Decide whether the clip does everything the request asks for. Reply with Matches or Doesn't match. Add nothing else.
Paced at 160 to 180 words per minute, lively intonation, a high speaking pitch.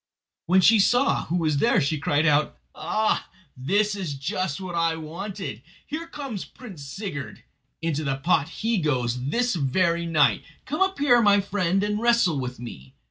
Doesn't match